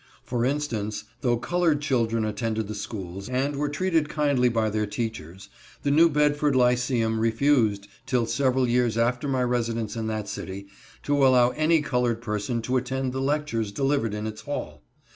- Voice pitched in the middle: No, low, 125 Hz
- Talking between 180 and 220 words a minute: No, average, 165 wpm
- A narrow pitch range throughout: No, average, 4.2 semitones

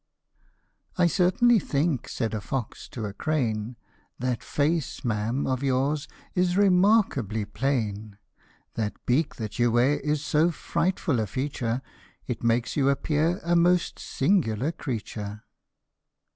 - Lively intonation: Yes, wide, 6.4 semitones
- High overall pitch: No, low, 135 Hz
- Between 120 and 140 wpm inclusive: Yes, slow, 135 wpm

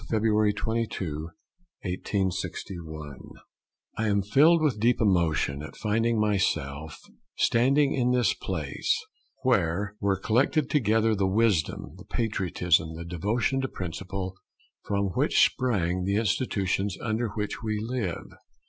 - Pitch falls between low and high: No, low, 105 Hz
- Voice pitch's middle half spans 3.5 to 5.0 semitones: Yes, average, 4.2 semitones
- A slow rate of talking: Yes, slow, 120 wpm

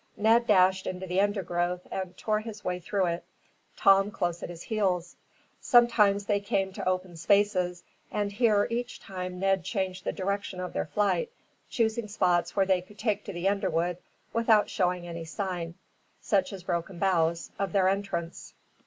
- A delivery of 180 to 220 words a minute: No, average, 170 wpm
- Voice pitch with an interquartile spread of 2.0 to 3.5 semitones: Yes, narrow, 2.4 semitones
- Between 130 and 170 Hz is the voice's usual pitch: No, high, 190 Hz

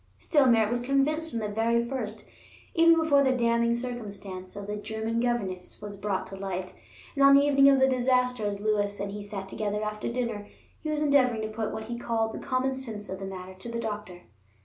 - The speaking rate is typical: No, fast, 215 wpm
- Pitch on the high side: Yes, high, 225 Hz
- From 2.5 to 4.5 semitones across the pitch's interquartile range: Yes, average, 3.8 semitones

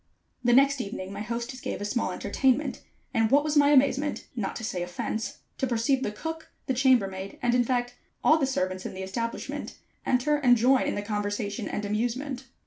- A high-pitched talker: Yes, high, 240 Hz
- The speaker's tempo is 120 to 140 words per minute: No, average, 200 wpm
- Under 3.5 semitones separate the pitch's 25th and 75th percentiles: No, average, 4.4 semitones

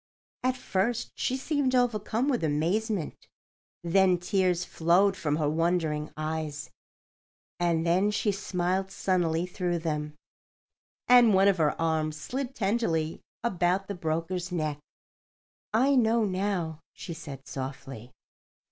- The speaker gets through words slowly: Yes, slow, 120 wpm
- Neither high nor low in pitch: Yes, medium, 180 Hz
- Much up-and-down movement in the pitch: No, average, 4.5 semitones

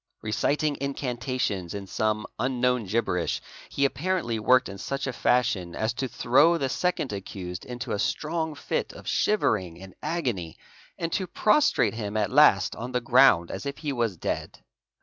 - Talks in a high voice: No, low, 125 Hz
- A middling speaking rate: Yes, average, 165 wpm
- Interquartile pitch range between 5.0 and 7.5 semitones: Yes, wide, 5.4 semitones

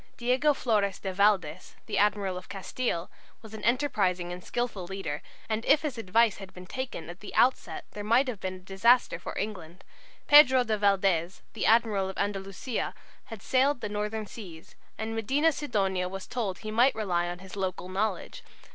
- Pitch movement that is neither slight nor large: Yes, average, 4.0 semitones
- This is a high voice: Yes, high, 205 Hz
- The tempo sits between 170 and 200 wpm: Yes, average, 180 wpm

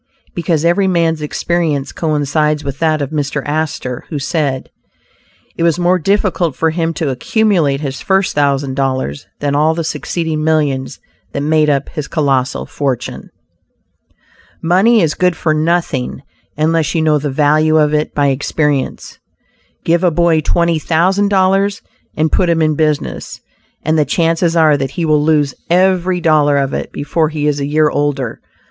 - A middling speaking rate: Yes, average, 165 wpm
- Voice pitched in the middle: Yes, medium, 155 Hz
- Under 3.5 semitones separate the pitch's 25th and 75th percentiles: Yes, average, 2.8 semitones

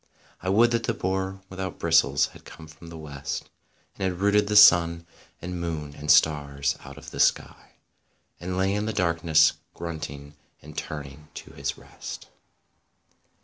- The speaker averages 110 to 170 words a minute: Yes, average, 160 wpm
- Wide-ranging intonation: No, average, 3.8 semitones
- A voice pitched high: No, very low, 85 Hz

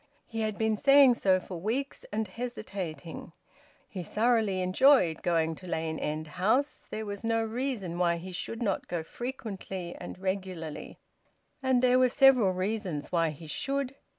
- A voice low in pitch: No, high, 200 Hz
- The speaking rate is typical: Yes, average, 155 wpm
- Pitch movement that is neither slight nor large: No, wide, 5.7 semitones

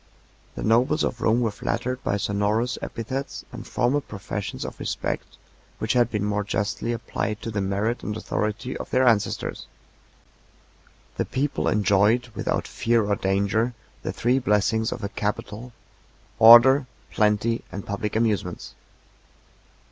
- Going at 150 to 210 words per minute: No, average, 140 wpm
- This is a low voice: Yes, low, 110 Hz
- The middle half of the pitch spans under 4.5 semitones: Yes, average, 2.8 semitones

